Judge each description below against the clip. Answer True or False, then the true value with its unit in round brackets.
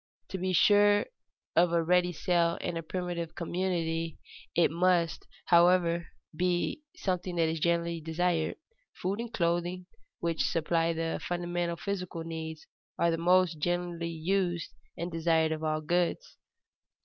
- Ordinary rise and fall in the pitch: False (1.4 semitones)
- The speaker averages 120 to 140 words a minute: True (135 wpm)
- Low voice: False (170 Hz)